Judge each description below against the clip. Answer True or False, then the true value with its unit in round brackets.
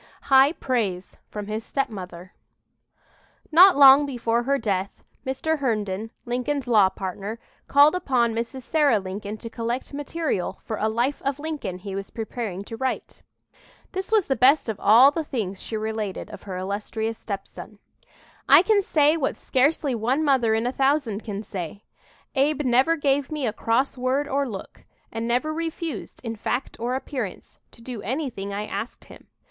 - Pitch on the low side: False (245 Hz)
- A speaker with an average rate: True (165 wpm)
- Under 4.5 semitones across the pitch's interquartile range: False (4.8 semitones)